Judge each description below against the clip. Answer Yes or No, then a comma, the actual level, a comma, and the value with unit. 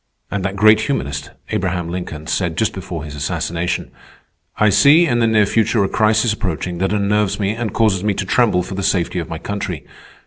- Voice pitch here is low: Yes, low, 100 Hz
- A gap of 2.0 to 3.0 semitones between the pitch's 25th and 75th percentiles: No, average, 3.5 semitones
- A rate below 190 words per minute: No, average, 200 wpm